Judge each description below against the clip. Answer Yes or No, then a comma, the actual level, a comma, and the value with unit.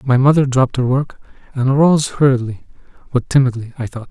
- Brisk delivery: No, average, 175 wpm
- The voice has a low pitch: Yes, low, 130 Hz